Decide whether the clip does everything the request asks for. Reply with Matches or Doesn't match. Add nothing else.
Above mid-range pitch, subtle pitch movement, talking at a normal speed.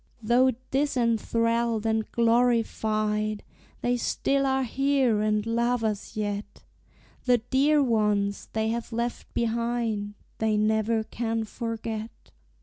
Doesn't match